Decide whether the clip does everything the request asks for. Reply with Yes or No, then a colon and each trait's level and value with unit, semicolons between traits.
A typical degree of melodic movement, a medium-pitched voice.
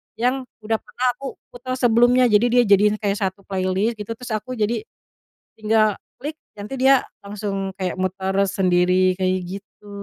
No: average, 4.2 semitones; high, 210 Hz